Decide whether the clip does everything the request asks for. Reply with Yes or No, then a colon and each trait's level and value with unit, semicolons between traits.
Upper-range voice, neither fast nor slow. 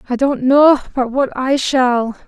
Yes: very high, 260 Hz; average, 185 wpm